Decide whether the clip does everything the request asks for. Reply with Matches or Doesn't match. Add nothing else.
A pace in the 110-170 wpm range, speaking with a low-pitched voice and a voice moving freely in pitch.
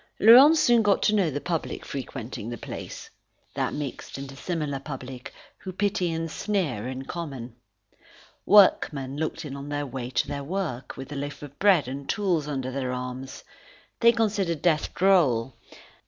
Doesn't match